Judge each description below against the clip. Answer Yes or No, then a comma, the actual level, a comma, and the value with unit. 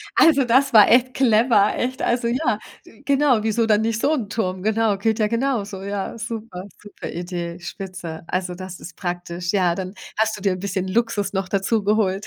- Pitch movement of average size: Yes, average, 3.7 semitones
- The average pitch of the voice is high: Yes, high, 210 Hz